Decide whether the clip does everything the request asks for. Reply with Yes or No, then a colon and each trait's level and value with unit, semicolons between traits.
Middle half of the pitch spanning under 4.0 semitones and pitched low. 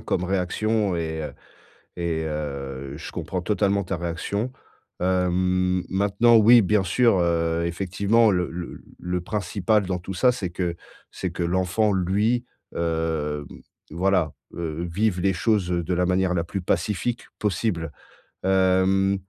Yes: average, 2.8 semitones; very low, 90 Hz